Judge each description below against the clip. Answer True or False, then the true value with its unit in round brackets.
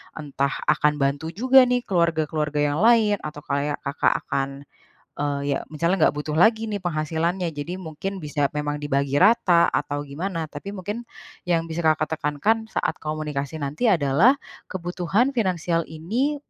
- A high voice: False (160 Hz)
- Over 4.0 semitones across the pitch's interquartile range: True (4.6 semitones)